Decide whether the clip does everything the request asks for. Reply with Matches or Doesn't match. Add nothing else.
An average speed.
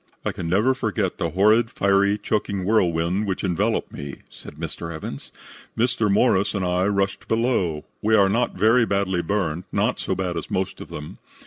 Matches